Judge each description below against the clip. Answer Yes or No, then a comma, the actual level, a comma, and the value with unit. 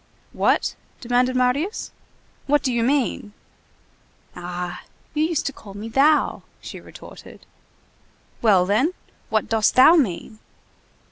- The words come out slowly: Yes, slow, 120 wpm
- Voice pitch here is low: No, high, 245 Hz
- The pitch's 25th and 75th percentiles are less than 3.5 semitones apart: No, average, 5.1 semitones